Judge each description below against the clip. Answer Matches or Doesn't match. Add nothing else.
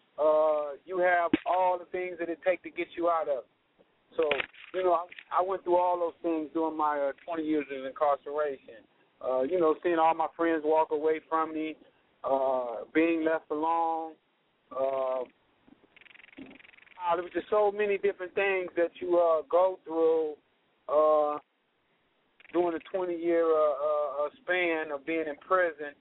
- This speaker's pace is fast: Doesn't match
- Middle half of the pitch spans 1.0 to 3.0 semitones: Matches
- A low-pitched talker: Doesn't match